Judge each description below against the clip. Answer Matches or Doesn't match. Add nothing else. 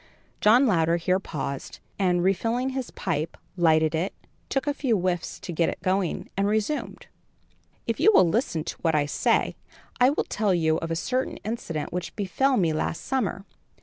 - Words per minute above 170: Matches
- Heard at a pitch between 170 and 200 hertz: Matches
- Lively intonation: Matches